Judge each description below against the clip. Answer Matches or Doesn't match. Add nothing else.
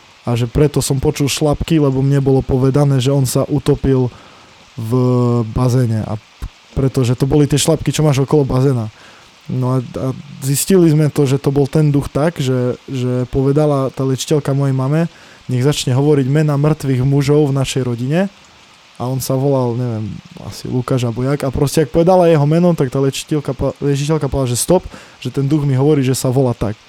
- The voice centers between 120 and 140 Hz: Matches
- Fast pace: Matches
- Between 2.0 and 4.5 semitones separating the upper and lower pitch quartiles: Matches